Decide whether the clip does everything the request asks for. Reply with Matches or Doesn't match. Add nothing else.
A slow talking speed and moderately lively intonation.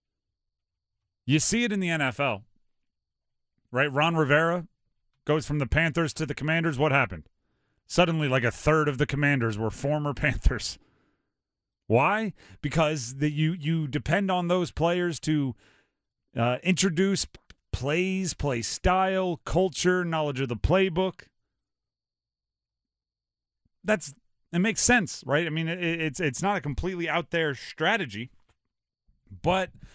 Doesn't match